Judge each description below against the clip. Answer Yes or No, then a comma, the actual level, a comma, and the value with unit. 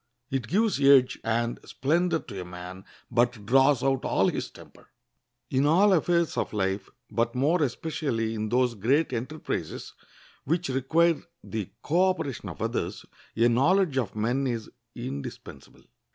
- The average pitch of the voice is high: No, low, 130 Hz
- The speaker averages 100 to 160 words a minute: Yes, average, 145 wpm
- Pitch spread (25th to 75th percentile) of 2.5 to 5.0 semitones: No, wide, 5.6 semitones